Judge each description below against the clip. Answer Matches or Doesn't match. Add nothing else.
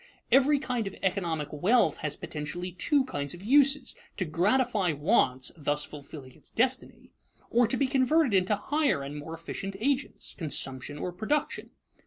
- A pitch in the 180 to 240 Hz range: Matches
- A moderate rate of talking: Matches